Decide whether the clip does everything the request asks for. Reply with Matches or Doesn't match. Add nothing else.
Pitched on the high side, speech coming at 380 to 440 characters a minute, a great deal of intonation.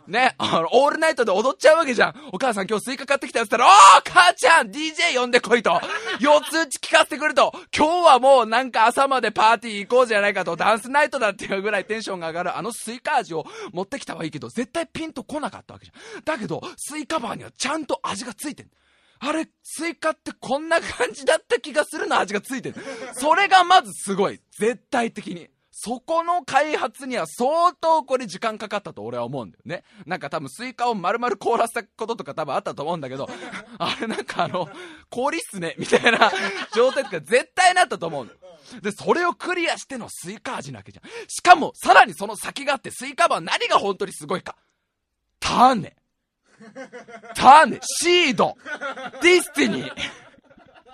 Matches